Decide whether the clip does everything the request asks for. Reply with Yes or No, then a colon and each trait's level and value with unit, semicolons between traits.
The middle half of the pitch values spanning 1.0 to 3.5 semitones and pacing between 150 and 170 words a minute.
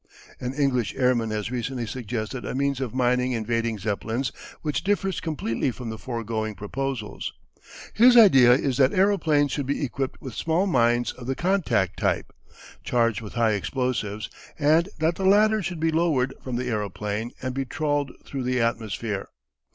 No: average, 4.1 semitones; average, 165 wpm